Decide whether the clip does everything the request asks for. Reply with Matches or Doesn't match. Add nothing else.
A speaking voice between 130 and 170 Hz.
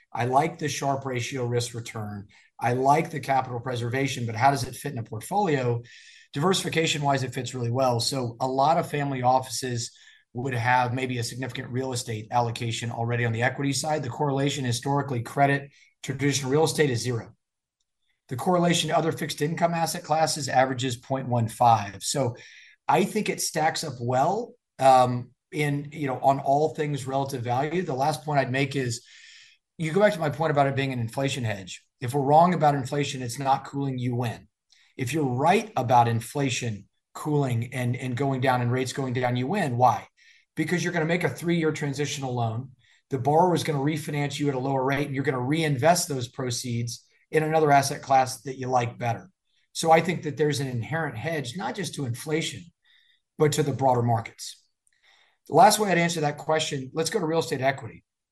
Matches